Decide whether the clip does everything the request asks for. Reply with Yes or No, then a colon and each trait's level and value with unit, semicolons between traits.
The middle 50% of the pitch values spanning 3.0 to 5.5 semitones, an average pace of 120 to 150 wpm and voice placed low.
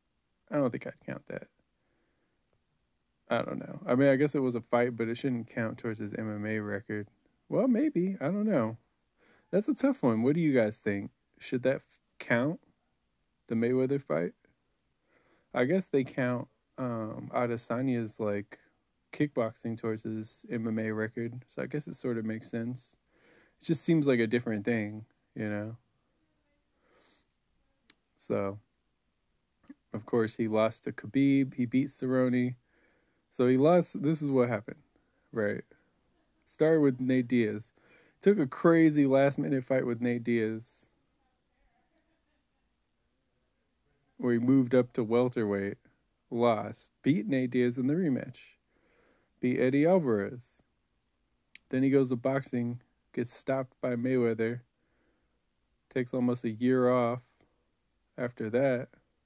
Yes: average, 3.3 semitones; average, 140 wpm; low, 120 Hz